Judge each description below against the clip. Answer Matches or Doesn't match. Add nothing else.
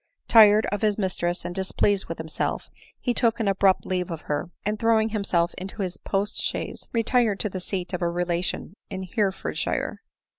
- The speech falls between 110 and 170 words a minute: Doesn't match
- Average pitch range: Matches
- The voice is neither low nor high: Doesn't match